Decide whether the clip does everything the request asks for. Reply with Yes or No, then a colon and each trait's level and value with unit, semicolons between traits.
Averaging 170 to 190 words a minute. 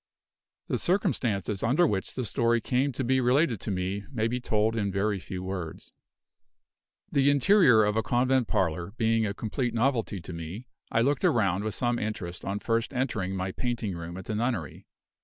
Yes: average, 180 wpm